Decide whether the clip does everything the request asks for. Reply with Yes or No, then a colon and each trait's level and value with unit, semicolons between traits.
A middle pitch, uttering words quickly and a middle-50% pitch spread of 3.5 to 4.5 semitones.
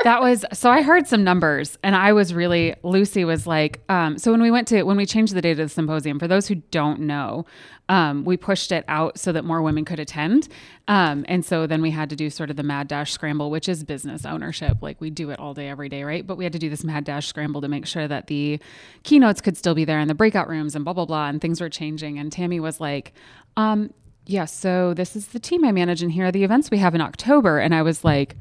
Yes: medium, 165 Hz; fast, 270 wpm; average, 4.2 semitones